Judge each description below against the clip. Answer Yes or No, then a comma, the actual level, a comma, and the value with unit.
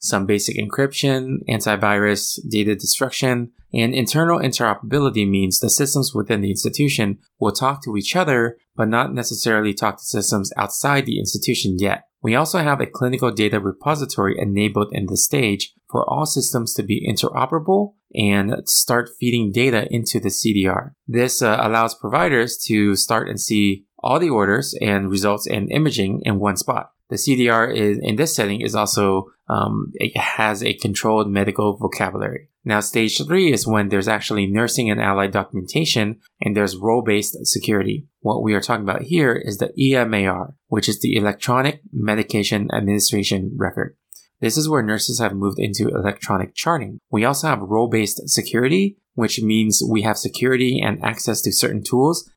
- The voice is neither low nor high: No, low, 110 Hz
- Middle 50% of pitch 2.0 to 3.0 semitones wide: No, average, 3.5 semitones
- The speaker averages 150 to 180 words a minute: Yes, average, 165 wpm